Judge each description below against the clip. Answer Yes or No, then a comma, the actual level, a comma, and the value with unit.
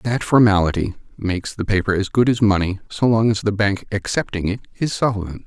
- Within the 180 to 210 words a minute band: Yes, average, 200 wpm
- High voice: No, low, 105 Hz